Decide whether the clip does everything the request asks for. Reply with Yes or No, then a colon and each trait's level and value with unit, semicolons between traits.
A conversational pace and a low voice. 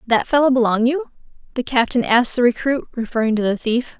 No: average, 195 wpm; high, 245 Hz